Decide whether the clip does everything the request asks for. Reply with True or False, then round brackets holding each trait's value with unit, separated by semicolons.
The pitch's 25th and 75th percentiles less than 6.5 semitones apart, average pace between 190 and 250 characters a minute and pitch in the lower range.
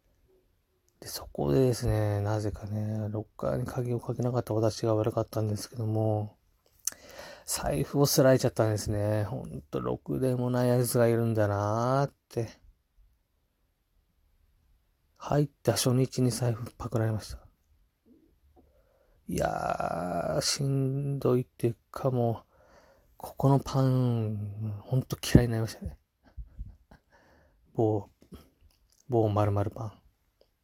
True (5.5 semitones; 235 characters per minute; 110 Hz)